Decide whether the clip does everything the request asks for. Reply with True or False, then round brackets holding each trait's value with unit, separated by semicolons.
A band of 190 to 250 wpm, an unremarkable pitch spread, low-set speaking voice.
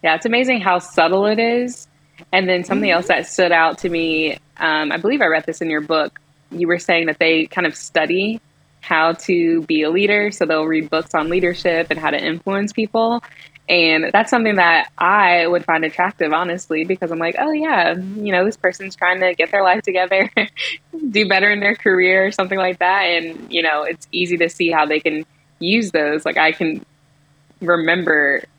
False (205 wpm; 3.2 semitones; 175 Hz)